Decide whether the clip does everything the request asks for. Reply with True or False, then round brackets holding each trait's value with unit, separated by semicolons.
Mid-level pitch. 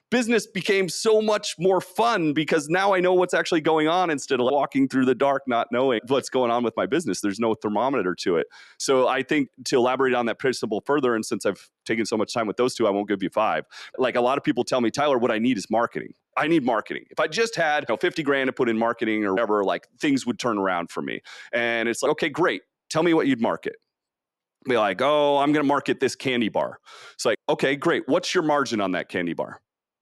True (150 Hz)